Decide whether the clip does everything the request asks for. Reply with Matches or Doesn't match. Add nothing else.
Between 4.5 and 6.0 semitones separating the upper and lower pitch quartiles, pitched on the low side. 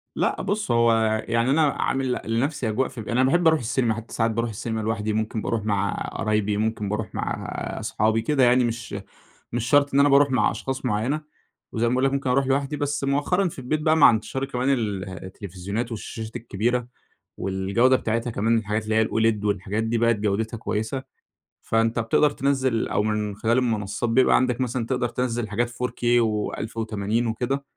Doesn't match